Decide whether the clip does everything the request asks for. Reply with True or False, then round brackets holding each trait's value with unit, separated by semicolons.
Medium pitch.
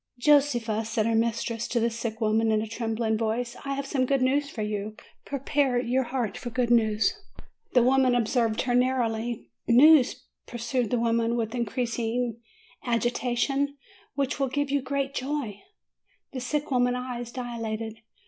False (240 Hz)